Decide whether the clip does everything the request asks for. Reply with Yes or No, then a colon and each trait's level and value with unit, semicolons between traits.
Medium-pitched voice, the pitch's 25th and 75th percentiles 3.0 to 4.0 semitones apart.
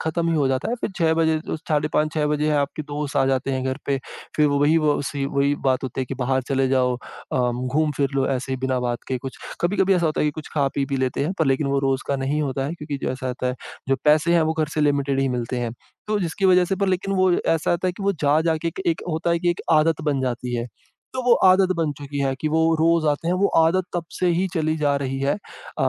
Yes: medium, 150 Hz; average, 3.6 semitones